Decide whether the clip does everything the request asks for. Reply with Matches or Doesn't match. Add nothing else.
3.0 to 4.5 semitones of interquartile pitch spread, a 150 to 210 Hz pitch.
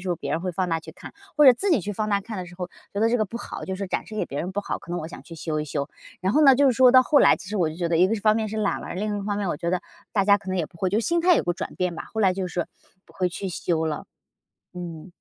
Matches